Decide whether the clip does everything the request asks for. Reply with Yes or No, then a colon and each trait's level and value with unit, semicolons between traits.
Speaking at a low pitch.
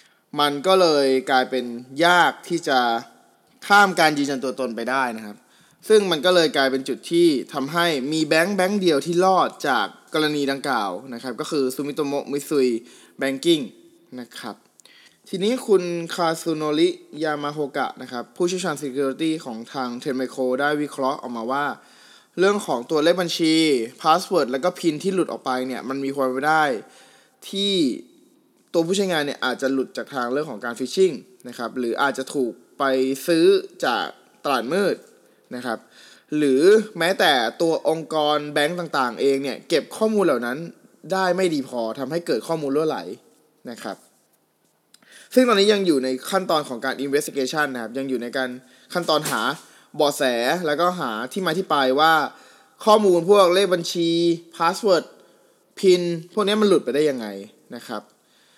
No: medium, 155 Hz